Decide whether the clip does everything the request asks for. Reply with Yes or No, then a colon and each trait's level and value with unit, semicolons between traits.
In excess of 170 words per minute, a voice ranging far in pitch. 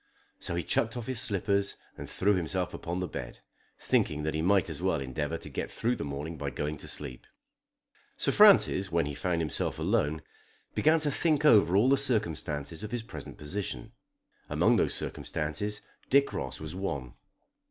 Yes: average, 180 wpm; wide, 6.2 semitones